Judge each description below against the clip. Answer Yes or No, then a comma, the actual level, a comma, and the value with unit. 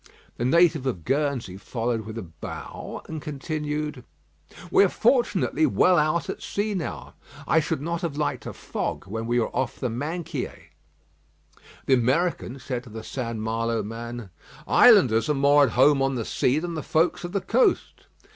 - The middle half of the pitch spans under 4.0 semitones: No, wide, 5.5 semitones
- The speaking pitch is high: No, low, 135 Hz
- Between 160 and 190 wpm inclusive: Yes, average, 175 wpm